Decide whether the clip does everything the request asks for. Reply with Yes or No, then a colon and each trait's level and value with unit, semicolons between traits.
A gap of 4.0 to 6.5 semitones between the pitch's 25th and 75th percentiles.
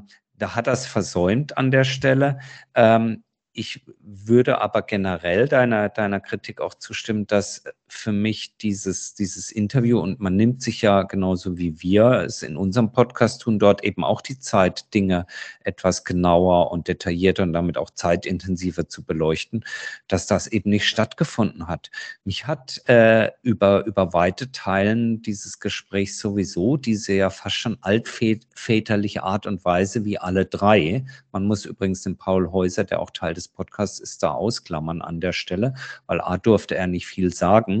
No: average, 3.3 semitones